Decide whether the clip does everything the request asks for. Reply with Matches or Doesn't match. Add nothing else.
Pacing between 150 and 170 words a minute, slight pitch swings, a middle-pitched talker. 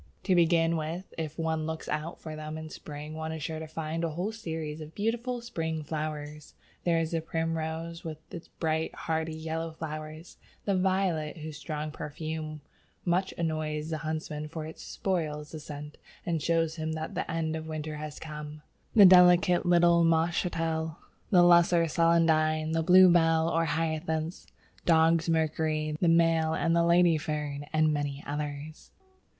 Matches